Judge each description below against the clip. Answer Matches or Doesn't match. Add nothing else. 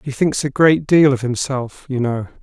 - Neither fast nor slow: Doesn't match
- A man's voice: Matches